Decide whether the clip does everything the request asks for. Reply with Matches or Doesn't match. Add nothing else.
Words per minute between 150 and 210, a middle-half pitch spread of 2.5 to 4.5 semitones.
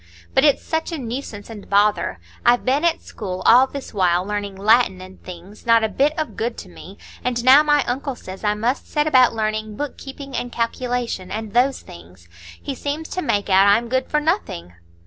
Doesn't match